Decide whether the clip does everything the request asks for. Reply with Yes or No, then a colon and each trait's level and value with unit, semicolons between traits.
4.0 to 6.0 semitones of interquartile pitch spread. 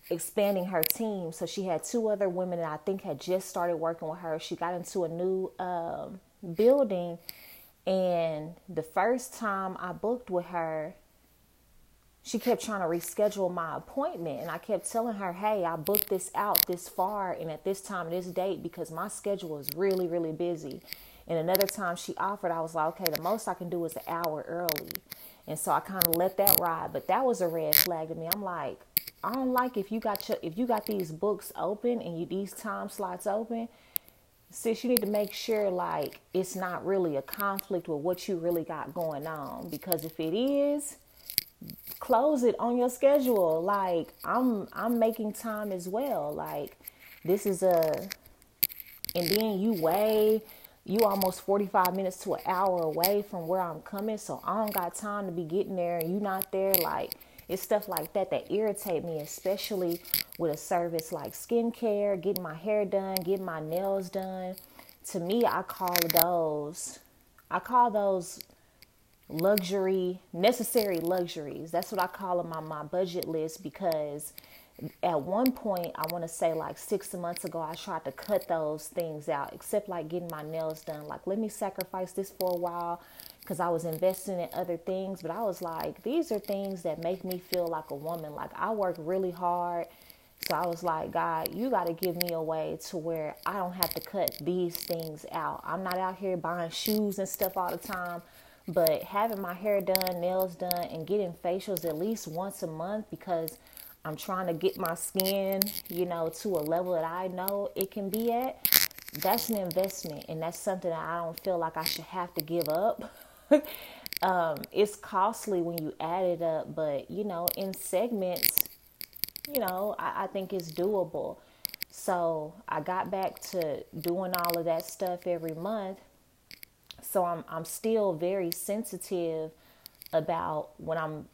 No: average, 3.1 semitones